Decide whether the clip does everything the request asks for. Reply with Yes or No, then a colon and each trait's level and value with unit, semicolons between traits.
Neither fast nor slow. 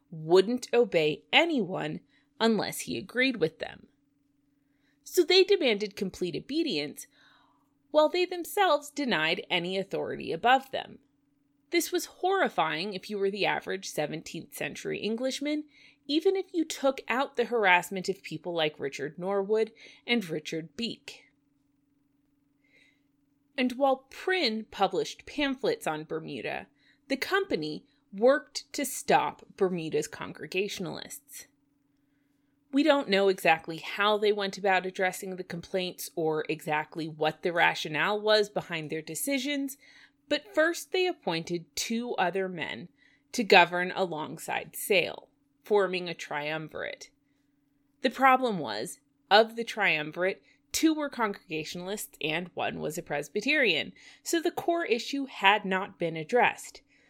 No: slow, 120 wpm